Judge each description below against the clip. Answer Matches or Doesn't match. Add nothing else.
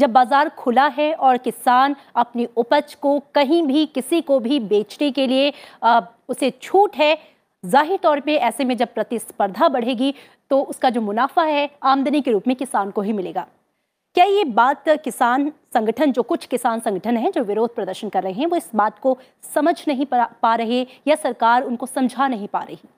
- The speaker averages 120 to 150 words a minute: Doesn't match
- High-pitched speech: Matches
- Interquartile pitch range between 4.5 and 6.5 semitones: Doesn't match